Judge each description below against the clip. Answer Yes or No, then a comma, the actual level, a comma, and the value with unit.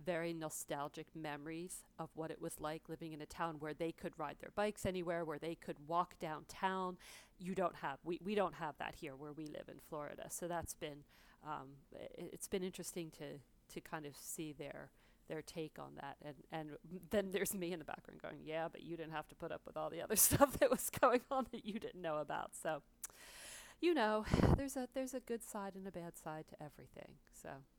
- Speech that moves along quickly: Yes, fast, 220 wpm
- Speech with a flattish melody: No, average, 3.6 semitones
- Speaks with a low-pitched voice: No, medium, 165 Hz